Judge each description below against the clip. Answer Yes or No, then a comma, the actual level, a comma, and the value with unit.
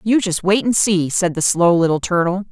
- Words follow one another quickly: Yes, fast, 240 wpm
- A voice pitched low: No, medium, 185 Hz